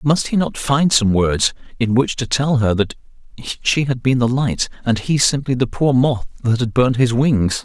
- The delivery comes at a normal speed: No, fast, 220 wpm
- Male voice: Yes, male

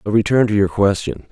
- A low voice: Yes, low, 105 Hz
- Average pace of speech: No, fast, 230 wpm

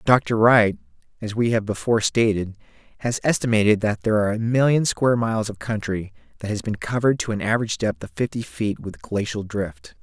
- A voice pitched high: No, low, 110 Hz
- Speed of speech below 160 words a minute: No, average, 180 wpm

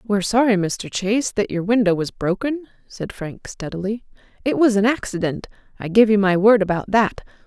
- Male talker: No, female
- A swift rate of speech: No, average, 185 wpm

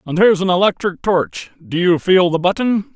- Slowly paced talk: No, fast, 205 wpm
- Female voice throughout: No, male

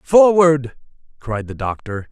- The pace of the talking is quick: No, slow, 115 wpm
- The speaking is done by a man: Yes, male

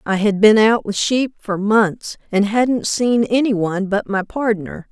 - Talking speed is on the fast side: No, average, 195 wpm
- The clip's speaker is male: No, female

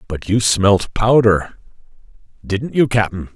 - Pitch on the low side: Yes, low, 105 Hz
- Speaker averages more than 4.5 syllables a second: No, 3.4 syllables/s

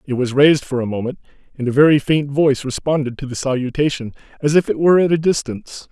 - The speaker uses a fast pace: Yes, fast, 225 wpm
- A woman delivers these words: No, male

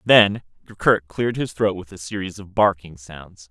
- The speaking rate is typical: Yes, average, 190 wpm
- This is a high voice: No, very low, 95 Hz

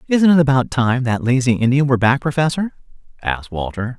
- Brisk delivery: No, average, 180 wpm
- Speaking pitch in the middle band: No, low, 130 Hz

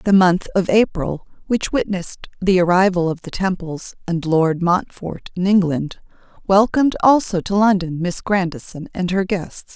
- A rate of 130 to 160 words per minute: Yes, average, 155 wpm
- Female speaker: Yes, female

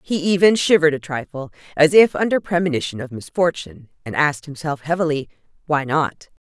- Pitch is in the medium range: Yes, medium, 155 Hz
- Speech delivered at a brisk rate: No, average, 160 wpm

